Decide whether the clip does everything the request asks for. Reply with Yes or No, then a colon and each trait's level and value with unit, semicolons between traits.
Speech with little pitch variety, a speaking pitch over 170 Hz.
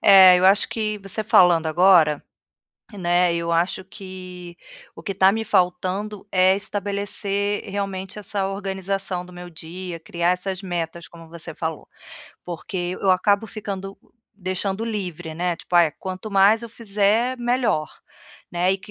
Yes: narrow, 2.3 semitones; high, 190 Hz